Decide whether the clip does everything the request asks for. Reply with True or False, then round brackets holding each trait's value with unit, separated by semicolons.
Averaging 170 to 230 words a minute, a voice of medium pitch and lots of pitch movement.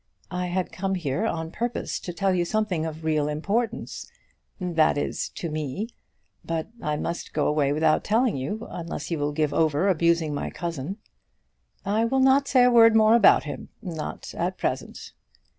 True (175 wpm; 175 Hz; 5.7 semitones)